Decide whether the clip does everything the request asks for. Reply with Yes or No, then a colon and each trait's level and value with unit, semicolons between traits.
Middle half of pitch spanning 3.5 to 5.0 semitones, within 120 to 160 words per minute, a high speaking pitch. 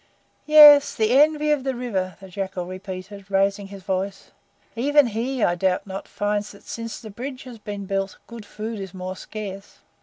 No: average, 4.0 semitones; average, 180 wpm; high, 205 Hz